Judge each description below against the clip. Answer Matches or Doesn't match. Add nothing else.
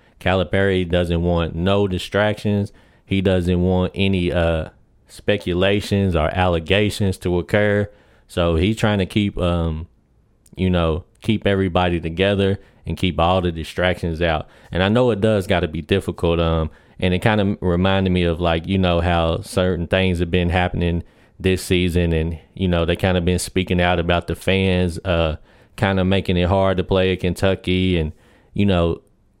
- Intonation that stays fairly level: Matches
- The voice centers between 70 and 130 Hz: Matches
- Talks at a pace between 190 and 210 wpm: Doesn't match